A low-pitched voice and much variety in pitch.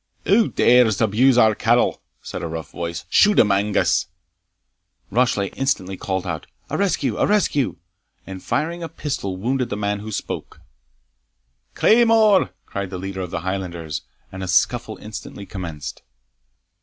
Yes: low, 105 Hz; wide, 6.1 semitones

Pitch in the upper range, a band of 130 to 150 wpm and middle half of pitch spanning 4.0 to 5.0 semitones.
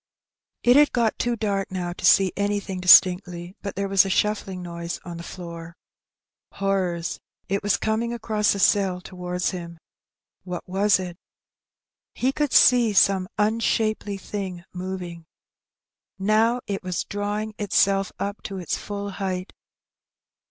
No: high, 195 Hz; average, 140 wpm; narrow, 2.6 semitones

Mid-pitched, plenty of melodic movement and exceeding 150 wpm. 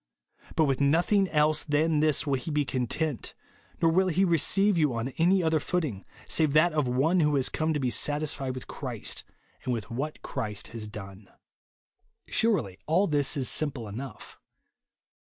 No: medium, 150 Hz; average, 4.1 semitones; average, 170 wpm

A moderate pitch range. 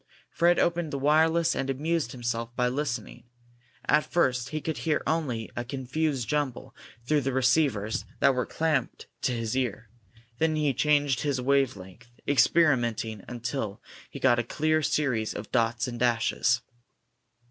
Yes: average, 4.1 semitones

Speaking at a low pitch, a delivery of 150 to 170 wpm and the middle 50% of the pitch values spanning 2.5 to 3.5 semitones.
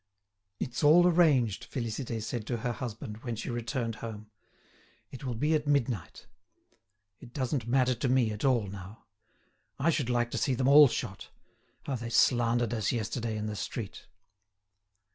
Yes: low, 120 Hz; average, 160 wpm; average, 3.0 semitones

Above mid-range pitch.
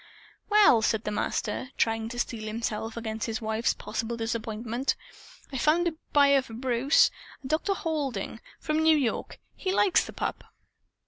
Yes: high, 235 Hz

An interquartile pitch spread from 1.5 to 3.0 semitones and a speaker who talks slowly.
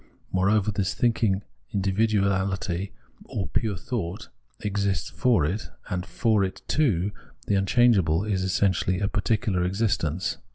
Yes: narrow, 2.5 semitones; slow, 120 wpm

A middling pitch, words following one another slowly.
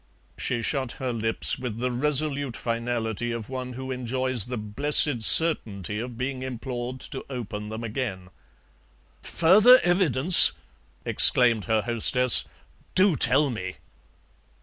No: low, 125 Hz; slow, 125 wpm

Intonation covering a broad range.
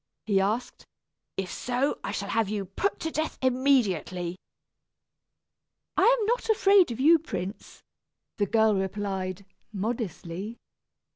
Yes: wide, 6.2 semitones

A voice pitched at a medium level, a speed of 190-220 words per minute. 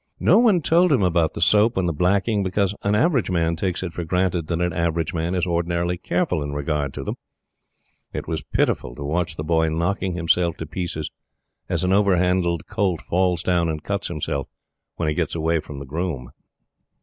No: very low, 85 Hz; average, 200 wpm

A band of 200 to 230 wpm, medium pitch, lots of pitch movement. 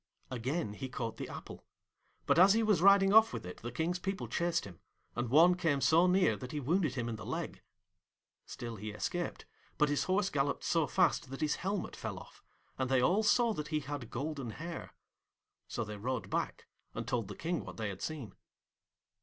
Yes: fast, 205 wpm; medium, 150 Hz; wide, 6.9 semitones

